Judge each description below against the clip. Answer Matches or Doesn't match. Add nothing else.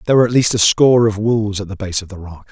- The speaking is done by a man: Matches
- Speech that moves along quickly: Matches